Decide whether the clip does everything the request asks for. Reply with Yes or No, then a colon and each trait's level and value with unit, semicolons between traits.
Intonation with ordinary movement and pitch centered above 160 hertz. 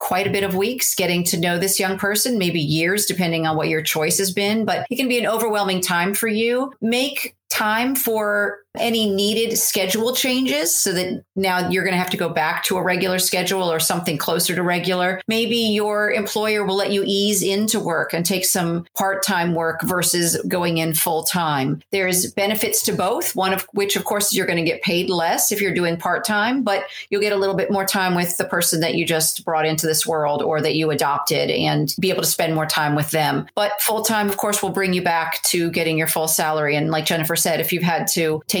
Yes: average, 3.7 semitones; medium, 185 Hz